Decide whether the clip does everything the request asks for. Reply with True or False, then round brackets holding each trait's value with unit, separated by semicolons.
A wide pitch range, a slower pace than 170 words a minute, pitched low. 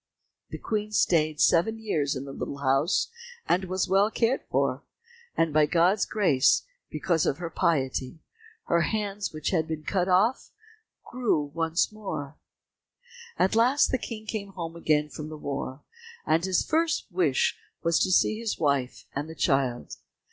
False (5.7 semitones; 160 wpm; 170 Hz)